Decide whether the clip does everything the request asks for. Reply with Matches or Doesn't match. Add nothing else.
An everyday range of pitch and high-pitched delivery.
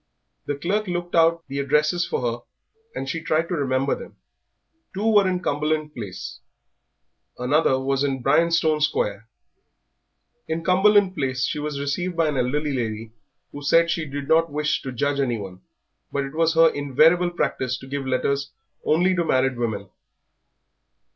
Doesn't match